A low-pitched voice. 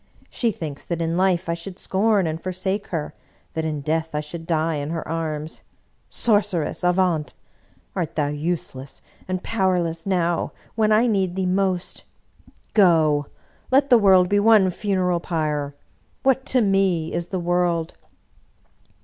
No: medium, 175 Hz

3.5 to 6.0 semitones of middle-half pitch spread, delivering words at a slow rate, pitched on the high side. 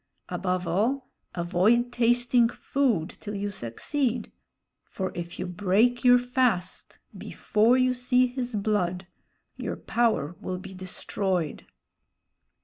Yes: average, 5.1 semitones; slow, 115 wpm; high, 210 Hz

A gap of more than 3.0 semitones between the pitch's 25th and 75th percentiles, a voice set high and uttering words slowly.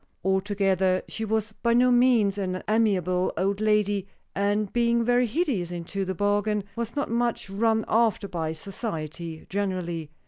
No: average, 3.4 semitones; high, 205 Hz; average, 145 wpm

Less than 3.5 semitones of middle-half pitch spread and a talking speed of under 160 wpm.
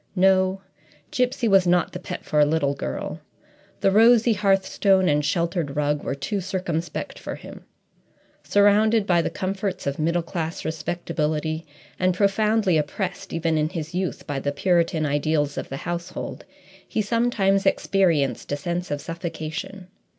No: average, 4.0 semitones; average, 150 wpm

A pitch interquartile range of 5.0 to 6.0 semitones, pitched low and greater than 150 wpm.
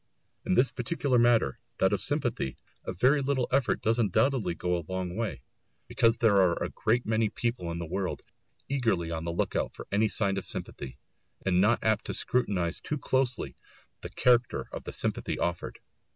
Yes: wide, 5.6 semitones; low, 110 Hz; average, 185 wpm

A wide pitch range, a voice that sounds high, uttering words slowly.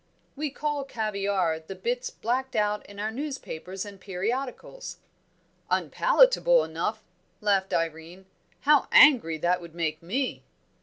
Yes: wide, 6.9 semitones; high, 210 Hz; slow, 120 wpm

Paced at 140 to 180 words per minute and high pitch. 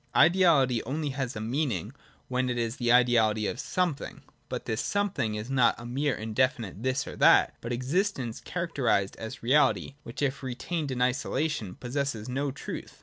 No: average, 165 wpm; low, 130 Hz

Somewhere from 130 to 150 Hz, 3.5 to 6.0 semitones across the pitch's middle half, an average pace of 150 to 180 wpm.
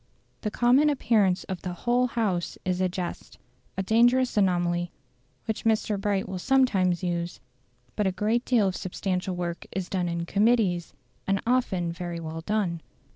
No: high, 190 Hz; average, 4.1 semitones; average, 160 wpm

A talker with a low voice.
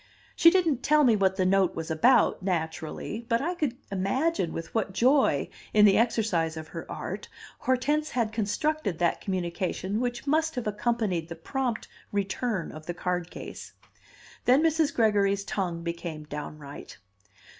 No: high, 205 Hz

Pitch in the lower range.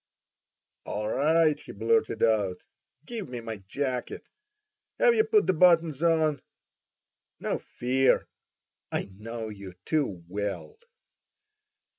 Yes: low, 130 Hz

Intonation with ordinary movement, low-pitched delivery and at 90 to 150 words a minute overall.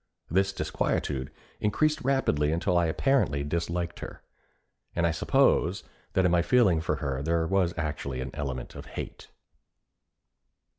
Yes: average, 4.3 semitones; very low, 85 Hz; average, 140 wpm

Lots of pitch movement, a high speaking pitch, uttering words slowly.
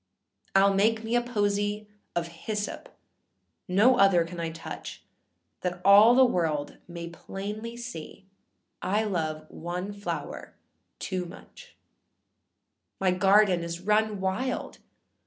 No: average, 3.4 semitones; high, 195 Hz; slow, 115 wpm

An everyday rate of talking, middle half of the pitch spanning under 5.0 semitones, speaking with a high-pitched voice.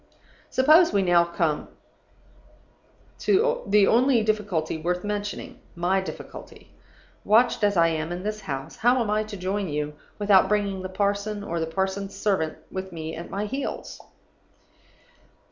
Yes: average, 145 wpm; average, 3.6 semitones; high, 195 Hz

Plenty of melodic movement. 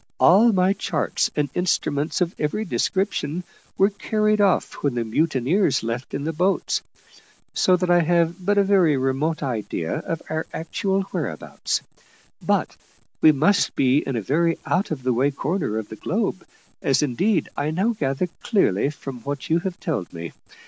Yes: wide, 5.8 semitones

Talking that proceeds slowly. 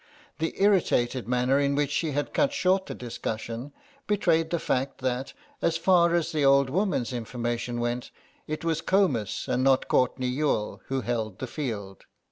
No: average, 165 wpm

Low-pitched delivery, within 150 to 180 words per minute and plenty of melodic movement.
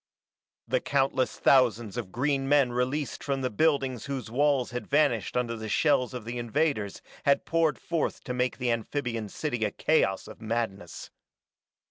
No: low, 125 Hz; average, 160 wpm; average, 3.4 semitones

